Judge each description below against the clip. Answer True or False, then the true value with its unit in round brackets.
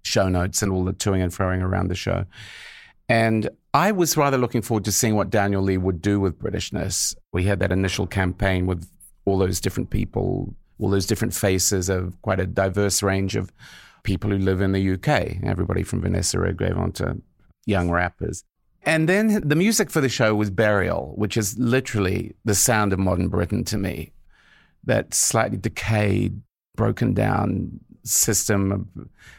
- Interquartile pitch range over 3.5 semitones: False (2.9 semitones)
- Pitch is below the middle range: True (100 Hz)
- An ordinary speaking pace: True (175 wpm)